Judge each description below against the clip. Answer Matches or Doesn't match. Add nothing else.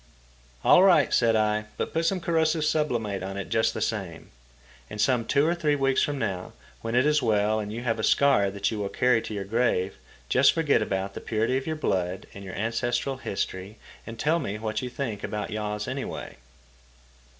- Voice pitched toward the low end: Matches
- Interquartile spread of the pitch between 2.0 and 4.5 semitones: Doesn't match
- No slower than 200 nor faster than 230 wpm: Matches